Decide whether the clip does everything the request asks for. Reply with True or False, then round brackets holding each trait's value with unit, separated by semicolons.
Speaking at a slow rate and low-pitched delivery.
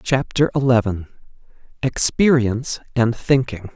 True (80 wpm; 120 Hz)